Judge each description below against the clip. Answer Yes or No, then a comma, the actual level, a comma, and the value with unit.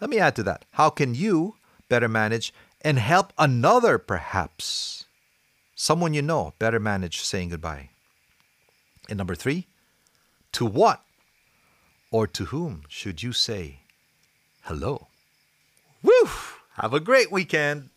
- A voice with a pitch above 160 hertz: No, low, 120 Hz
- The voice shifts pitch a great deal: Yes, wide, 7.7 semitones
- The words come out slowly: Yes, slow, 125 wpm